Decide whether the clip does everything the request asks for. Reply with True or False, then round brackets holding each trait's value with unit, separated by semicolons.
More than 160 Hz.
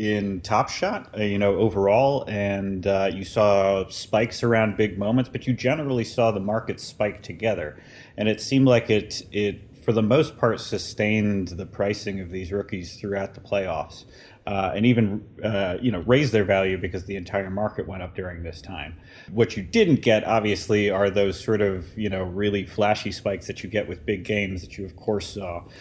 False (100 Hz)